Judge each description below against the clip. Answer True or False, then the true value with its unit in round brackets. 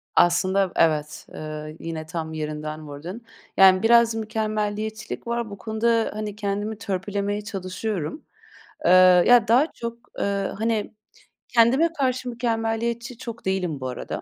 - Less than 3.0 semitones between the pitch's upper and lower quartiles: False (4.7 semitones)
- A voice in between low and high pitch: False (210 Hz)